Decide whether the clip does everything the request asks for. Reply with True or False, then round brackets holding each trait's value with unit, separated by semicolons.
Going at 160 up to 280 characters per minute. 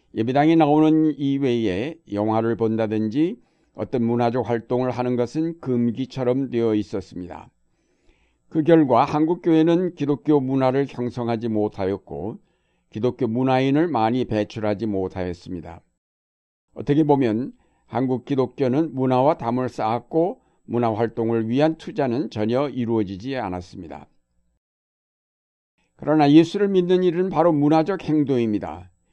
False (295 characters per minute)